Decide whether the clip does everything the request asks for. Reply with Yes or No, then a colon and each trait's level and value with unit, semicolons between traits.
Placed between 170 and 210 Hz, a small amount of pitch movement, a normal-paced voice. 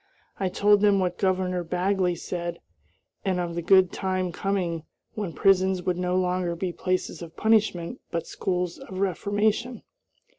Yes: medium, 185 Hz; narrow, 1.8 semitones; average, 150 wpm